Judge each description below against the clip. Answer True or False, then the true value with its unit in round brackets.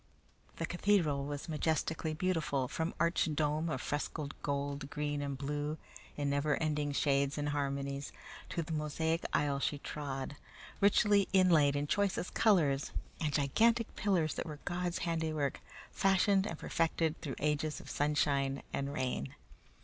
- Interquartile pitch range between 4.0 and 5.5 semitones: False (2.8 semitones)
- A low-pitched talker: False (150 Hz)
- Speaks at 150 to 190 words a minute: False (140 wpm)